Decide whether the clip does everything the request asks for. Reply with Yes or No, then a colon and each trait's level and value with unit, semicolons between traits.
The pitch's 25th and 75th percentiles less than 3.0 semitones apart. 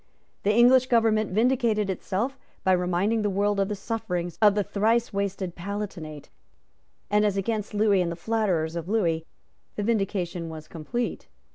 No: average, 3.5 semitones